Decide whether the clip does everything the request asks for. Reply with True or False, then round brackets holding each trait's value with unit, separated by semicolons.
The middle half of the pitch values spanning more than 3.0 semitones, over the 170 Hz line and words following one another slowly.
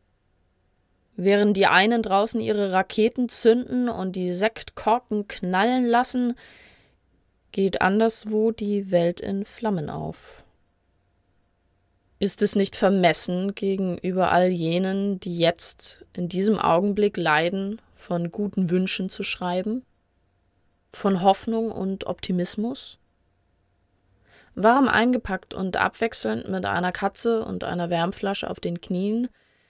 True (4.2 semitones; 190 Hz; 110 wpm)